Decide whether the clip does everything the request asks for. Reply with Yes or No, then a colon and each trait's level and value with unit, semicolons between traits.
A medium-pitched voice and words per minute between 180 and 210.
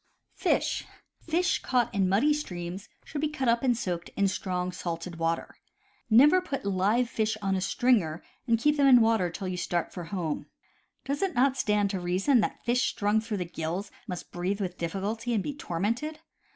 No: high, 205 Hz; average, 185 wpm